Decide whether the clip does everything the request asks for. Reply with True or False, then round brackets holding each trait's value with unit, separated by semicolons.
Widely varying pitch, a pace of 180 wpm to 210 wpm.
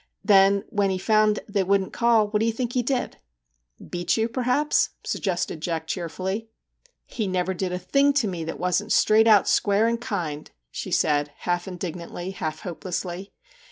False (4.0 semitones; 190 wpm)